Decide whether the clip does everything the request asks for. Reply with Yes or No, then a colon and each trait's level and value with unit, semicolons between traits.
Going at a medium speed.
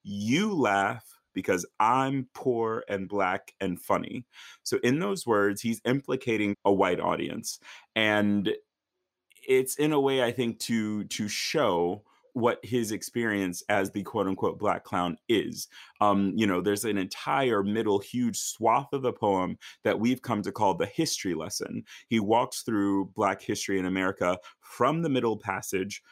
Yes: average, 160 wpm